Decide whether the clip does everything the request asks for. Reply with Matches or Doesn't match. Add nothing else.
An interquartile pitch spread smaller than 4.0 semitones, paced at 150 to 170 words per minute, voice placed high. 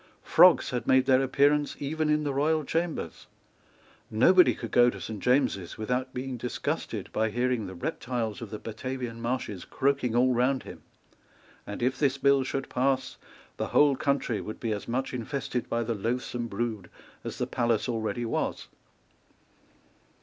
Doesn't match